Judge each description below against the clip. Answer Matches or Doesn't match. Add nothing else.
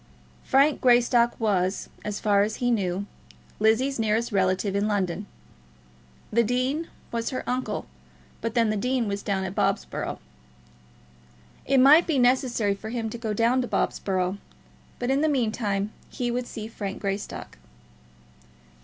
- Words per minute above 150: Doesn't match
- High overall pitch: Matches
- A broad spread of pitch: Doesn't match